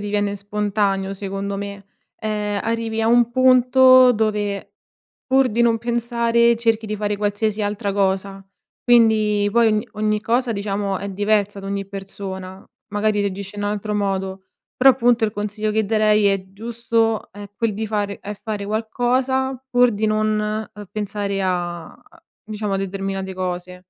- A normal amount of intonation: No, narrow, 2.2 semitones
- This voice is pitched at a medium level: No, high, 210 Hz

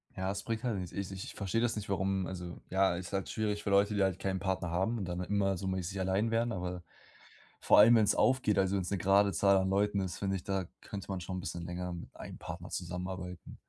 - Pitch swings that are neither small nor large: No, narrow, 1.8 semitones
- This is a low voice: Yes, very low, 95 Hz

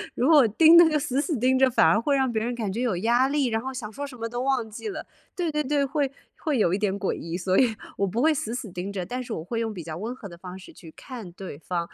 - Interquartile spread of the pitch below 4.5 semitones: No, wide, 5.4 semitones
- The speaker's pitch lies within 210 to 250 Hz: Yes, high, 235 Hz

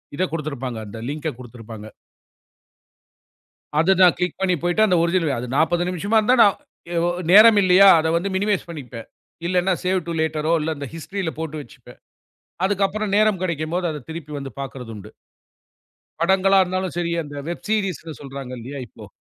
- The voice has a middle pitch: Yes, medium, 170 Hz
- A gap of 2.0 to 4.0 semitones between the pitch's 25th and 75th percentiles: No, average, 4.7 semitones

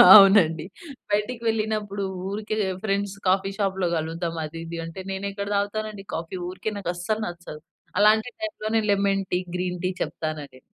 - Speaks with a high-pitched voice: Yes, high, 195 Hz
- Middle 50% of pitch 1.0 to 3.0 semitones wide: No, average, 3.4 semitones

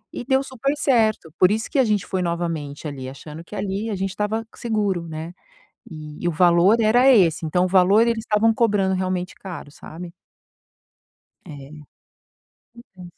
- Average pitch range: Yes, average, 4.6 semitones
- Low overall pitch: No, high, 190 Hz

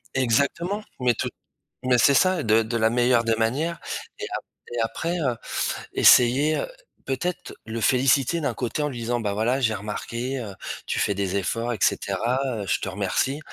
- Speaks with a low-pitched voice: Yes, low, 120 Hz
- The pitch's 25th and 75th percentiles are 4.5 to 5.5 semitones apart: No, average, 3.5 semitones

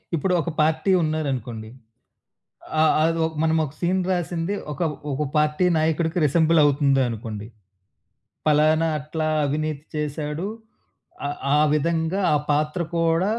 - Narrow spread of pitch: Yes, narrow, 2.0 semitones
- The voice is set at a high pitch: No, medium, 155 Hz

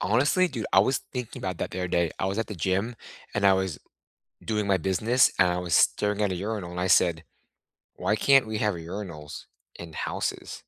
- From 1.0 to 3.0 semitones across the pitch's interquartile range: No, average, 3.6 semitones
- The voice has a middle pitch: No, very low, 95 Hz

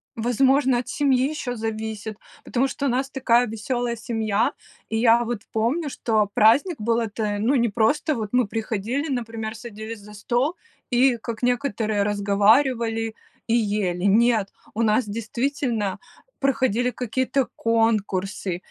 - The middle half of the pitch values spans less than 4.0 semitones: Yes, average, 2.7 semitones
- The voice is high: Yes, high, 230 Hz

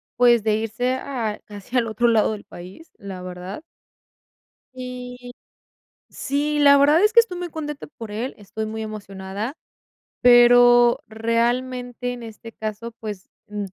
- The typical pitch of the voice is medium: No, high, 235 Hz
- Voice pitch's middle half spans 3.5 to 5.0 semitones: No, average, 2.9 semitones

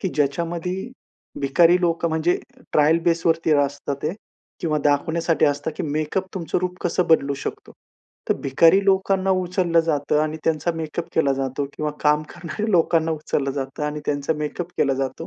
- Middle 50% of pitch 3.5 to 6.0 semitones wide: No, average, 2.9 semitones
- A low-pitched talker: No, medium, 160 Hz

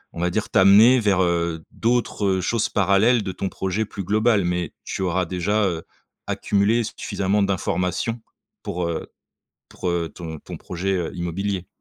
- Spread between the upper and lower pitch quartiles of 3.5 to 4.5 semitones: No, average, 3.0 semitones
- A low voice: Yes, very low, 95 Hz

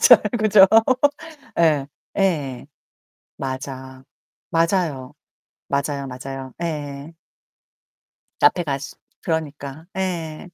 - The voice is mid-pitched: Yes, medium, 145 Hz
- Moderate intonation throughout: Yes, average, 3.7 semitones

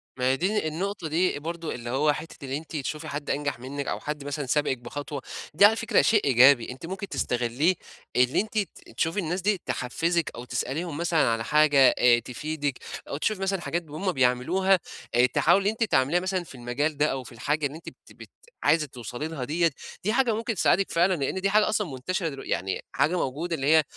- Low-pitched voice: No, medium, 155 Hz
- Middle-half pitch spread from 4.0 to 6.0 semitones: Yes, average, 5.2 semitones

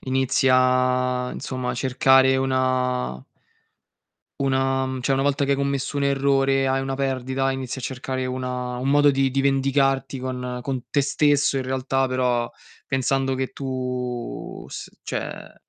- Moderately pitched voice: No, low, 130 Hz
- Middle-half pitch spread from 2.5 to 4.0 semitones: No, narrow, 1.0 semitones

